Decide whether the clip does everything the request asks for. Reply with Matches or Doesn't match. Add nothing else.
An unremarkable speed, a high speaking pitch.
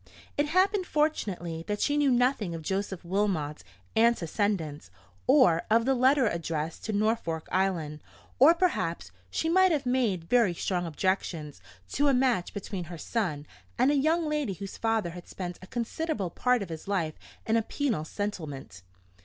Matches